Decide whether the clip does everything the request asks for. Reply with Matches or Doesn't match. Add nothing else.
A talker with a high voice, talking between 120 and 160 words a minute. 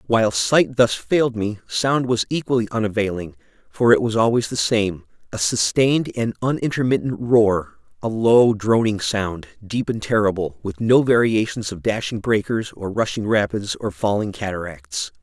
Doesn't match